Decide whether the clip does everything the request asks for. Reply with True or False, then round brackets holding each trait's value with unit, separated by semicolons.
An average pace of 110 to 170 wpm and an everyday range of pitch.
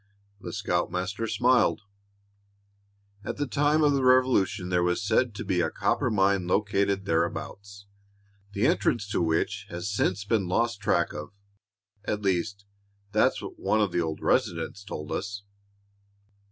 True (145 wpm; 3.6 semitones)